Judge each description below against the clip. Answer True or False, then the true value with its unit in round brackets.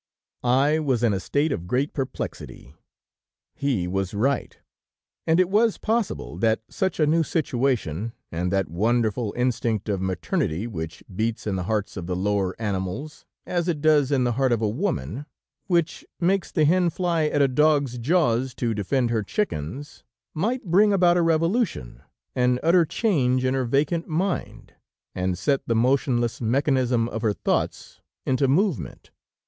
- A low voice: True (130 Hz)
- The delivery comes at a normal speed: True (160 wpm)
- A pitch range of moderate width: False (6.5 semitones)